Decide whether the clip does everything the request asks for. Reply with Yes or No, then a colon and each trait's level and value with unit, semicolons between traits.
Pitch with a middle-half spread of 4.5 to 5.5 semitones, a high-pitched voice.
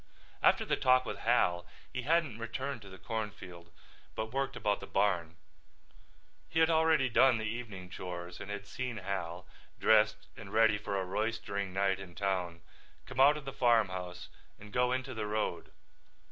No: average, 4.8 semitones; low, 105 Hz